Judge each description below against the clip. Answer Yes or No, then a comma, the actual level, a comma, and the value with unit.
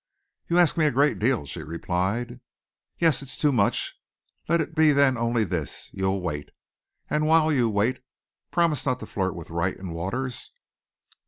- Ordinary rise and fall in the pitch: No, wide, 7.8 semitones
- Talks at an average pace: Yes, average, 170 wpm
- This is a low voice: Yes, low, 120 Hz